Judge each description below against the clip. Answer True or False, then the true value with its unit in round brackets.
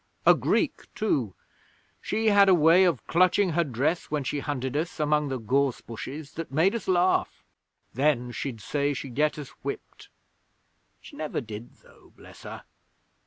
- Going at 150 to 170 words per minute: True (165 wpm)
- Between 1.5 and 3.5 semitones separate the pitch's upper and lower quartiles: False (4.4 semitones)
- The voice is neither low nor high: True (150 Hz)